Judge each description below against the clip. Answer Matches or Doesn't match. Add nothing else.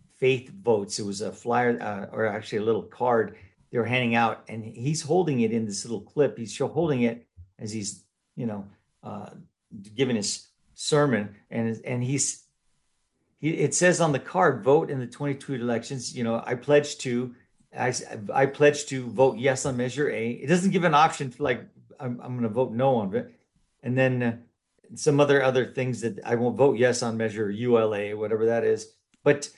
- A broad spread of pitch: Doesn't match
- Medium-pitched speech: Doesn't match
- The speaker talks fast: Doesn't match